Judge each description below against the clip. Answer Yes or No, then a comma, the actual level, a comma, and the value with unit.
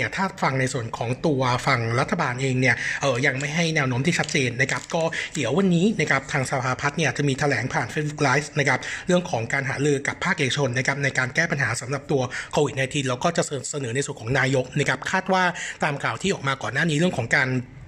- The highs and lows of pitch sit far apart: No, average, 3.4 semitones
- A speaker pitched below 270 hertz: Yes, medium, 140 Hz